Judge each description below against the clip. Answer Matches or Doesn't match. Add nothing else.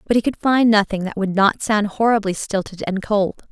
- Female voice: Matches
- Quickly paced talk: Matches